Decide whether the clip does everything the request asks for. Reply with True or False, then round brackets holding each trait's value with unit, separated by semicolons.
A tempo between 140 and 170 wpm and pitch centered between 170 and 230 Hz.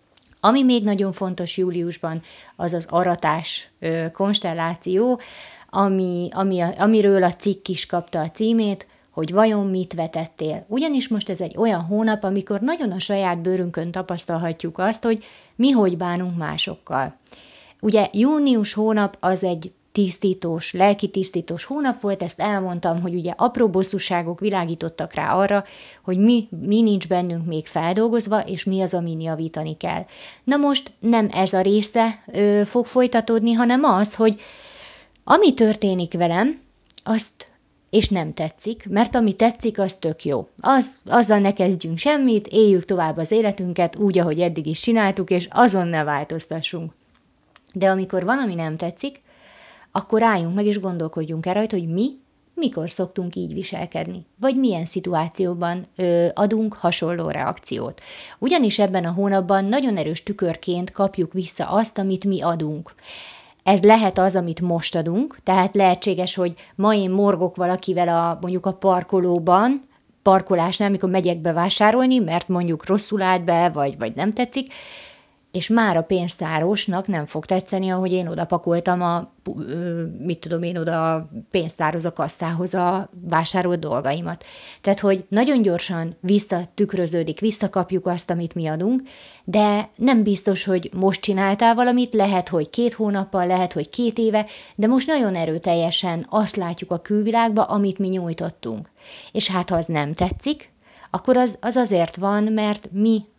True (145 wpm; 190 Hz)